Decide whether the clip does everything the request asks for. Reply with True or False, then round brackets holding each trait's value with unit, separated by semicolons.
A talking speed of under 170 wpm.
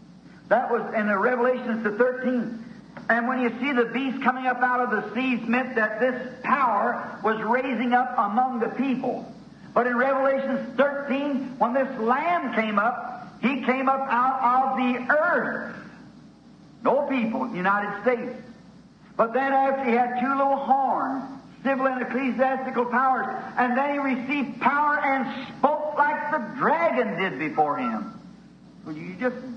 True (155 wpm)